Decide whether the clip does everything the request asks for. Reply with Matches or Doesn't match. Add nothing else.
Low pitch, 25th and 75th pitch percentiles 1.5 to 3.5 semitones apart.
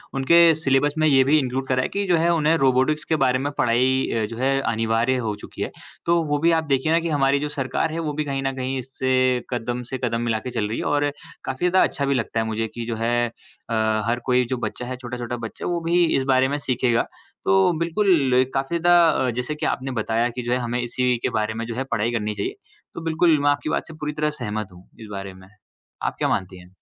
Doesn't match